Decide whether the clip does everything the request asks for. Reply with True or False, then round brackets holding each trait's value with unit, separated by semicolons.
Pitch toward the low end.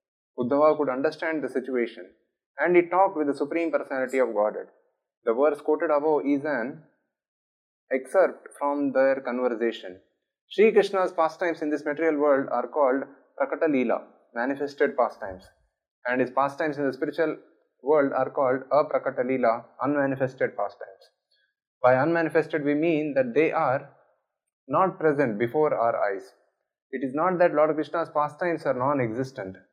False (145 Hz)